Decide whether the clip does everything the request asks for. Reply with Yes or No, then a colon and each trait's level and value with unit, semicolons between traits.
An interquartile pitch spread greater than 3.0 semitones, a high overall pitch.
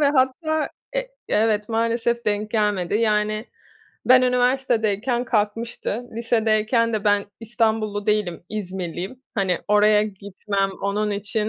No: narrow, 2.4 semitones; high, 215 Hz